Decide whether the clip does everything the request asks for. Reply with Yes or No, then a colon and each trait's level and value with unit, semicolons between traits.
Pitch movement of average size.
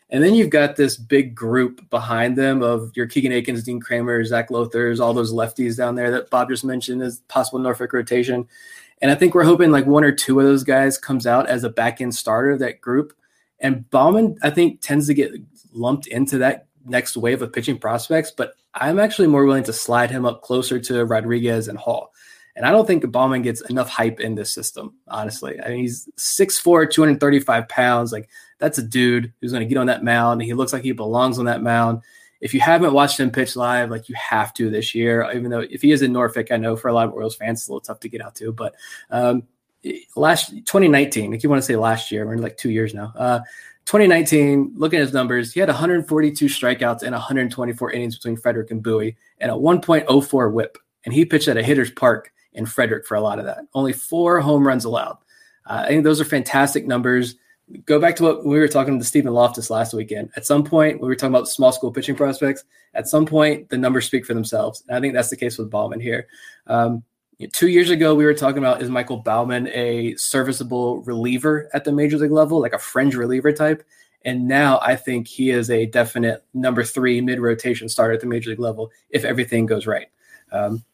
Yes: average, 3.2 semitones